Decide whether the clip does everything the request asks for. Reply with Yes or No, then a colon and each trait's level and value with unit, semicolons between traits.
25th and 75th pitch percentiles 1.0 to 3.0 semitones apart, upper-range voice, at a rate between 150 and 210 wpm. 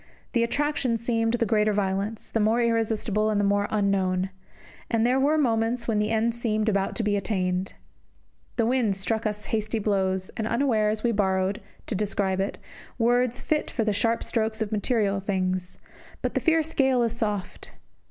Yes: narrow, 2.6 semitones; high, 215 Hz; average, 175 wpm